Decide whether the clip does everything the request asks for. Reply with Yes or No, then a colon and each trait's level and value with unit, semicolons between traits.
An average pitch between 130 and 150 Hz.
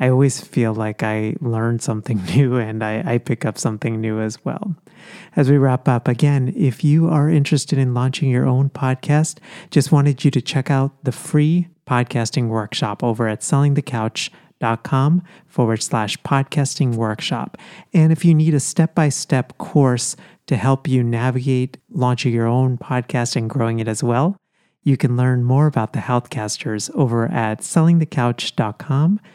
Yes: low, 135 Hz